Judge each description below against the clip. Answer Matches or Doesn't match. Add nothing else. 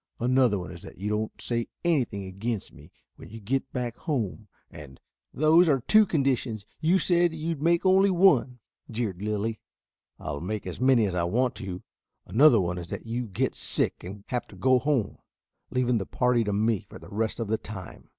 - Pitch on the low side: Matches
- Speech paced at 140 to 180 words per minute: Doesn't match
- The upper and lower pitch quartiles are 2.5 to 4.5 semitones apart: Doesn't match